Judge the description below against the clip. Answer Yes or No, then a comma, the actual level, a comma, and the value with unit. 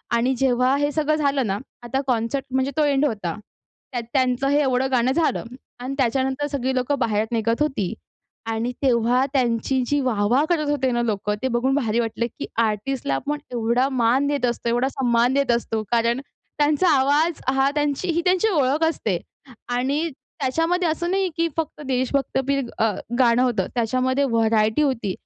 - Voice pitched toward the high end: Yes, very high, 260 Hz